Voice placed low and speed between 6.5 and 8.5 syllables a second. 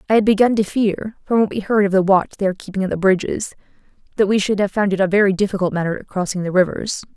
No: high, 195 Hz; 6.8 syllables/s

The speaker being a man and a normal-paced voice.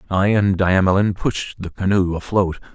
Yes: male; average, 155 wpm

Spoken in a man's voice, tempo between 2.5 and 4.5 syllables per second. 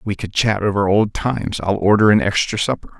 No: male; 5.6 syllables/s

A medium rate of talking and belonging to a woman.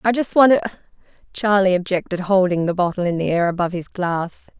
Yes: average, 195 wpm; female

